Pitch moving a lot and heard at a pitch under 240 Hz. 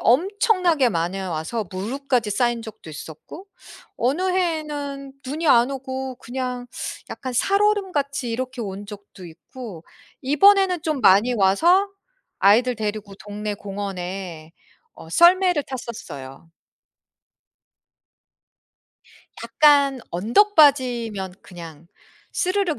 No: wide, 7.0 semitones; high, 245 Hz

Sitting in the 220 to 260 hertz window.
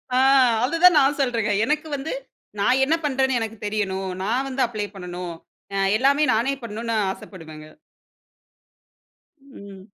Yes: high, 230 Hz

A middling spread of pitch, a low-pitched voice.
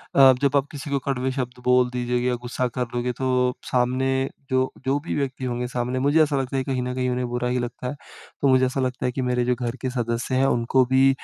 No: narrow, 1.2 semitones; low, 125 Hz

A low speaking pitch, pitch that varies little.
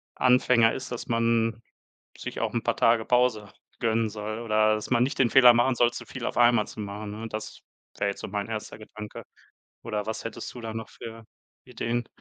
Yes: low, 115 Hz; narrow, 1.9 semitones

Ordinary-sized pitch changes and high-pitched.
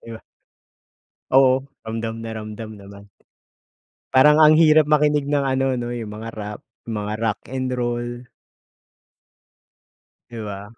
No: average, 3.6 semitones; low, 120 Hz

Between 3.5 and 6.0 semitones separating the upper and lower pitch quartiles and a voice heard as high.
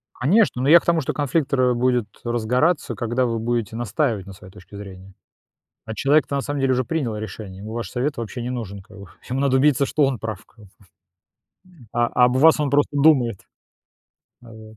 No: average, 4.1 semitones; low, 125 Hz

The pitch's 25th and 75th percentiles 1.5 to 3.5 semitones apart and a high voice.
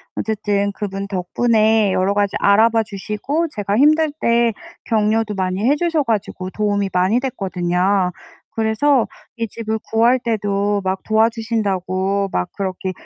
Yes: average, 2.7 semitones; high, 210 Hz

